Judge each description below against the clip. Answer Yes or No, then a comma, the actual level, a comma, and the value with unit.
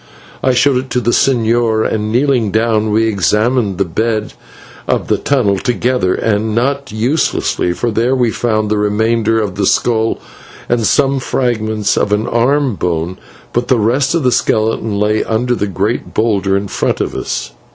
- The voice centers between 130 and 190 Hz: No, low, 110 Hz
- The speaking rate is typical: Yes, average, 170 wpm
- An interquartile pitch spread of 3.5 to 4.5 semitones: No, average, 2.7 semitones